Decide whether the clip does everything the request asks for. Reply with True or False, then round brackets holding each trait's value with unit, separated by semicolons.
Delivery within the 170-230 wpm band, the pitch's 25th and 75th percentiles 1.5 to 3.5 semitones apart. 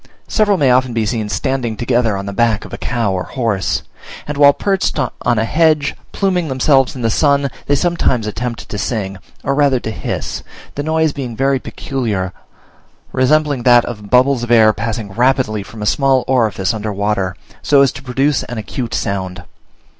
False (185 wpm; 4.3 semitones)